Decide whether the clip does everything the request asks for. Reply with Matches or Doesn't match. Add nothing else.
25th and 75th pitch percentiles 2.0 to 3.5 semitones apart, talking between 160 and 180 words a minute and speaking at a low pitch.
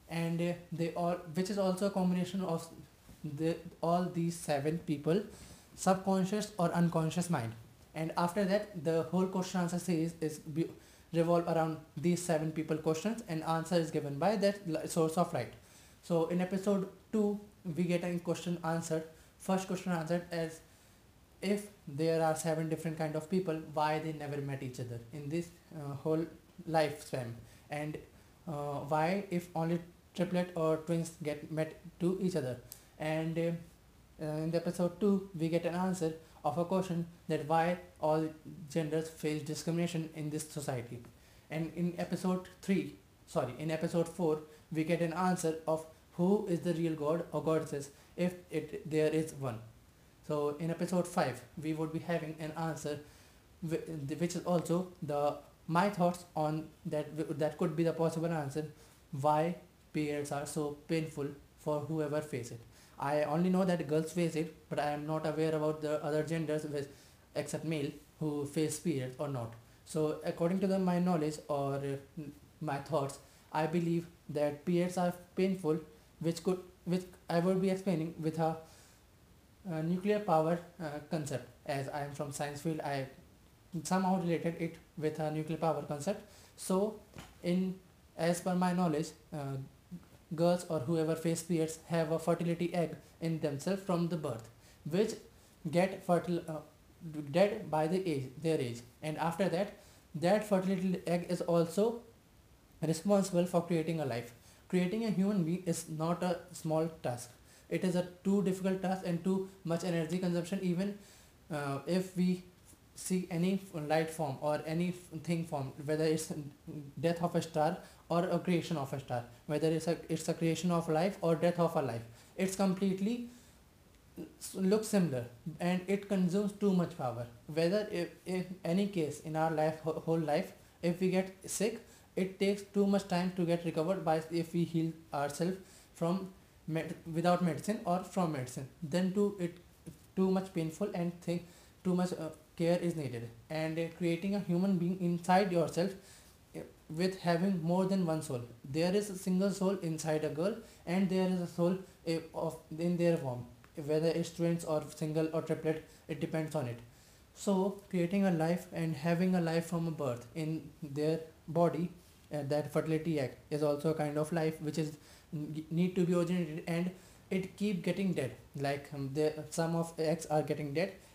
Doesn't match